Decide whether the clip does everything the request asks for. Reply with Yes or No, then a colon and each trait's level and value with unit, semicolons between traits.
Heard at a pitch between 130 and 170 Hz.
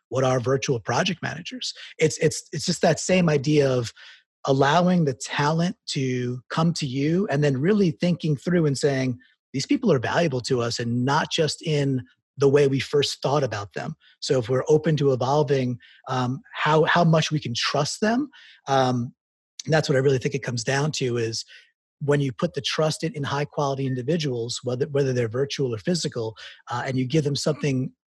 Yes: medium, 140 Hz